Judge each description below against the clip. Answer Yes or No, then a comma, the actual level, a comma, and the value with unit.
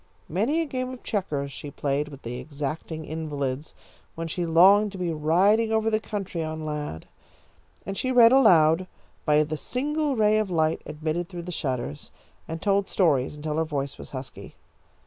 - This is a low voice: No, medium, 165 Hz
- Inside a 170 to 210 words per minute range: Yes, average, 175 wpm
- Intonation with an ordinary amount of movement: No, wide, 5.7 semitones